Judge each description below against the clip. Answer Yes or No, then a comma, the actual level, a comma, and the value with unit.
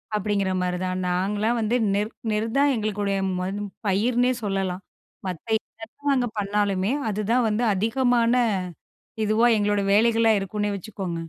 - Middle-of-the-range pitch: No, high, 210 Hz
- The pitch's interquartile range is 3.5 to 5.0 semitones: No, average, 2.8 semitones